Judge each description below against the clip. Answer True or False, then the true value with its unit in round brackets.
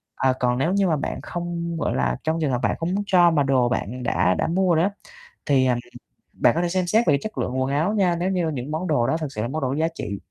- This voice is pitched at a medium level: True (155 Hz)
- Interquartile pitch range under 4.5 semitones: False (5.3 semitones)